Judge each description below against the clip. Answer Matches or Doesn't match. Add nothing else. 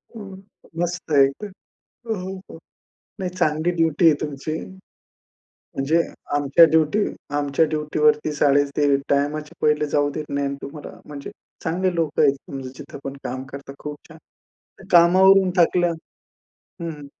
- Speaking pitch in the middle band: Matches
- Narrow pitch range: Doesn't match